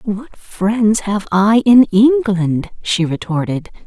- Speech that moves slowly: Yes, slow, 125 wpm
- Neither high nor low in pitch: No, high, 205 Hz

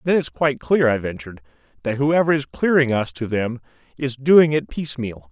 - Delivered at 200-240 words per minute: No, average, 190 wpm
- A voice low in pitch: Yes, low, 130 Hz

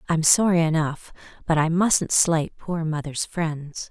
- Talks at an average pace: Yes, average, 155 wpm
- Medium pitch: Yes, medium, 160 Hz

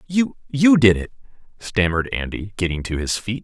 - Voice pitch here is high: No, low, 110 Hz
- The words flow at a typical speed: Yes, average, 155 wpm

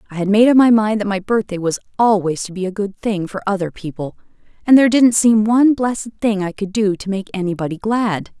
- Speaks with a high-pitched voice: Yes, high, 205 Hz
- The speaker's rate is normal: No, fast, 235 wpm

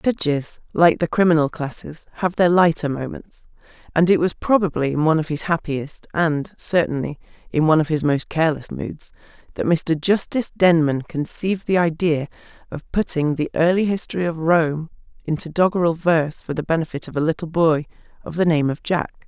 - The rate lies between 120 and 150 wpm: No, average, 175 wpm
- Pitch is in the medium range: Yes, medium, 160 Hz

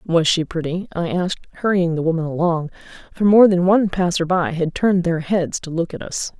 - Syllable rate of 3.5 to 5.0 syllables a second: No, 5.6 syllables/s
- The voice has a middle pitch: Yes, medium, 175 Hz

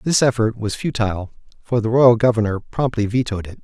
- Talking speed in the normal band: Yes, average, 180 wpm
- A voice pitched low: Yes, low, 115 Hz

